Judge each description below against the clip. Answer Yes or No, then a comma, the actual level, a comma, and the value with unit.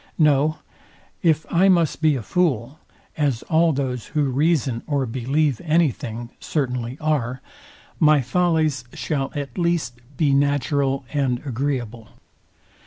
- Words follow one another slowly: Yes, slow, 125 wpm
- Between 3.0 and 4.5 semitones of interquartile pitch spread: Yes, average, 3.7 semitones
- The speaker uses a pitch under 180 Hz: Yes, medium, 140 Hz